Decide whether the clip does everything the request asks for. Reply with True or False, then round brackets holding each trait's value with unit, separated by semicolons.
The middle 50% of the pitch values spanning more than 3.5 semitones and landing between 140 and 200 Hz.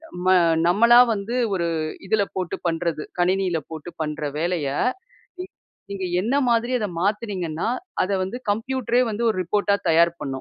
True (4.3 semitones; 190 Hz)